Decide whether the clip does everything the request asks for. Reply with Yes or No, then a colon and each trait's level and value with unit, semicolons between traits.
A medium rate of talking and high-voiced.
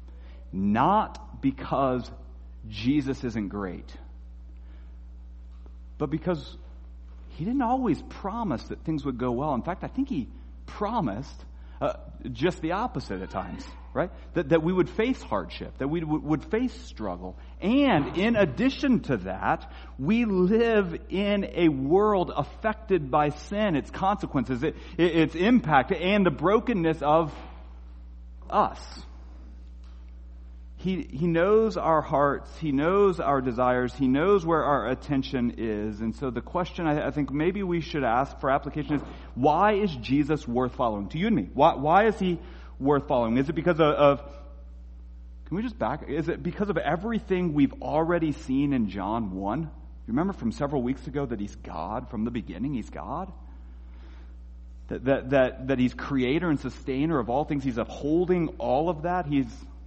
No: average, 160 wpm; medium, 140 Hz